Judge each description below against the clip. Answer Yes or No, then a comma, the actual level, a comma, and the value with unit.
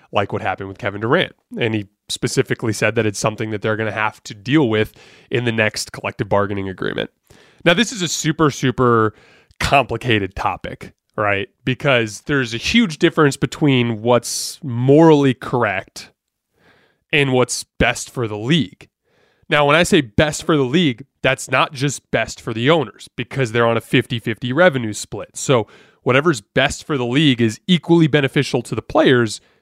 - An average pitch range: Yes, average, 4.6 semitones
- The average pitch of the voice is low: Yes, low, 125 Hz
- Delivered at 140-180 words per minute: Yes, average, 175 wpm